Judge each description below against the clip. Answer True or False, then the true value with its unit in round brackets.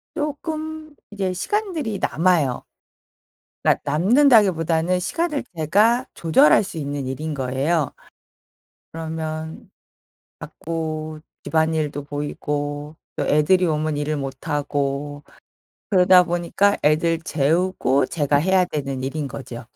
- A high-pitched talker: False (160 Hz)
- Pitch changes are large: False (4.2 semitones)